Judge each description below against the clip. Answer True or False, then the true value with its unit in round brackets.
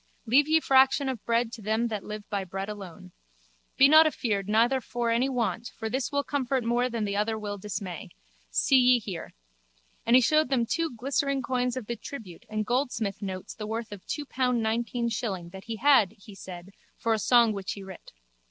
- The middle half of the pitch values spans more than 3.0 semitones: True (3.8 semitones)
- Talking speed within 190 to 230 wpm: True (200 wpm)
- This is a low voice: False (230 Hz)